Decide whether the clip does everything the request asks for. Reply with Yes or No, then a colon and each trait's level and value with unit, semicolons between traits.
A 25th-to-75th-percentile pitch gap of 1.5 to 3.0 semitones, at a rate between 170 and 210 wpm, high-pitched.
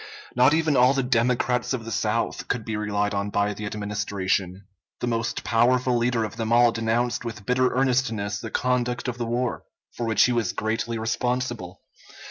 No: average, 2.7 semitones; average, 180 wpm; low, 115 Hz